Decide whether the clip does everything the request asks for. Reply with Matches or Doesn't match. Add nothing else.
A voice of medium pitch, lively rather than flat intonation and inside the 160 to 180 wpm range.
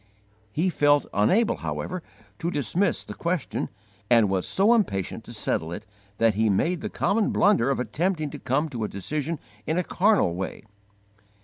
Matches